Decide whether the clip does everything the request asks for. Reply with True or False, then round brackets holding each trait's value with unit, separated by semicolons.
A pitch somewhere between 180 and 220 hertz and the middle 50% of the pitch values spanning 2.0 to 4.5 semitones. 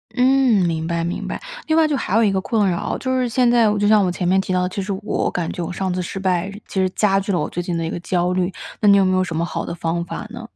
True (190 Hz; 3.5 semitones)